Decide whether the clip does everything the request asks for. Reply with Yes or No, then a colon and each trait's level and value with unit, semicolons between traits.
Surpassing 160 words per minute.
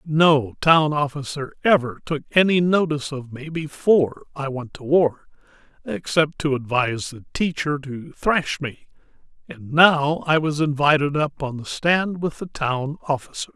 No: average, 155 wpm